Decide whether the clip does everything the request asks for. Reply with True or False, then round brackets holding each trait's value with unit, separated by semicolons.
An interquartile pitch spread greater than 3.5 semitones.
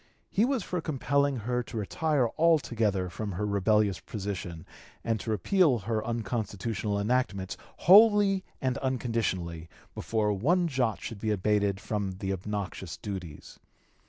True (4.9 semitones)